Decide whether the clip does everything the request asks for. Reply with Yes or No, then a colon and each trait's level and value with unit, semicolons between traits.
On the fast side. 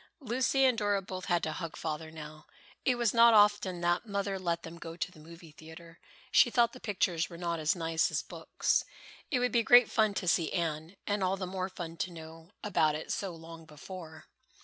Yes: fast, 215 wpm